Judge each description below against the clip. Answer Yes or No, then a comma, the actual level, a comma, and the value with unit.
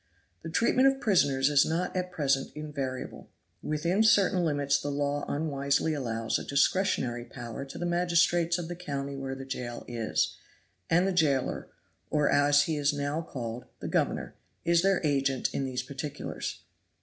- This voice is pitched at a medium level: Yes, medium, 145 Hz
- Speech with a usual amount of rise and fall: Yes, average, 4.0 semitones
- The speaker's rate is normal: Yes, average, 160 wpm